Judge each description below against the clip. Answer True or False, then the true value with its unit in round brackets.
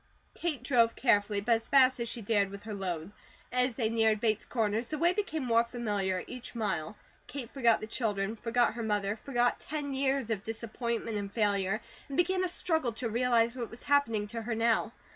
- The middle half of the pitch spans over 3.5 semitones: False (3.0 semitones)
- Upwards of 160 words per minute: True (200 wpm)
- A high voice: True (230 Hz)